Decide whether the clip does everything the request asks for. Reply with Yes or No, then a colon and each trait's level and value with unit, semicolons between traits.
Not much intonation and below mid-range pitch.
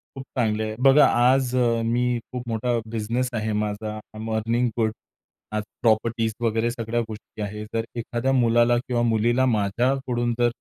Yes: narrow, 2.0 semitones; low, 115 Hz